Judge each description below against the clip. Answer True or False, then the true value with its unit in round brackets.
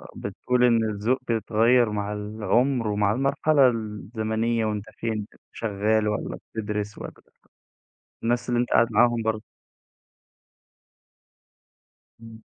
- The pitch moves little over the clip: True (2.1 semitones)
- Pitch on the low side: True (110 Hz)